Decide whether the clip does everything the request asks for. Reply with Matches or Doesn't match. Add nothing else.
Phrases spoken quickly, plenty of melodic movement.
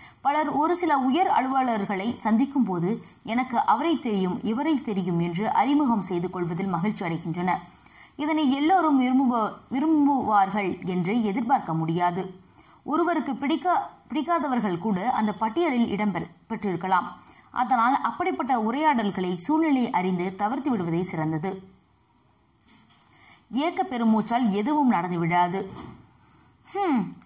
Doesn't match